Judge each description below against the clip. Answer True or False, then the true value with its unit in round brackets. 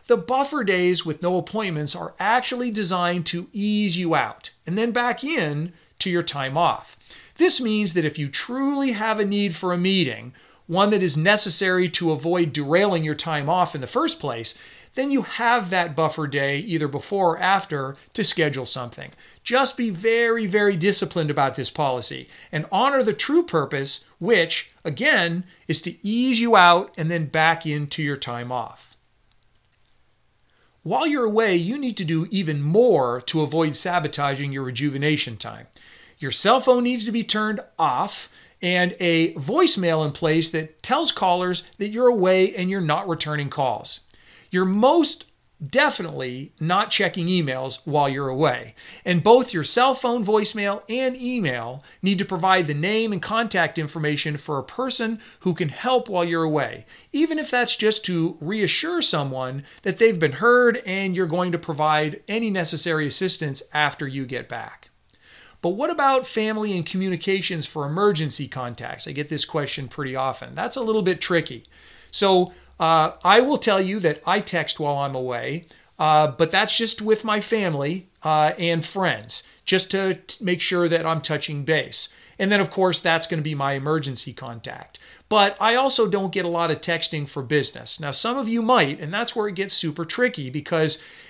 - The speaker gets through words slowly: False (175 wpm)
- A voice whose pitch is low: False (175 Hz)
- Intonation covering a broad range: True (5.8 semitones)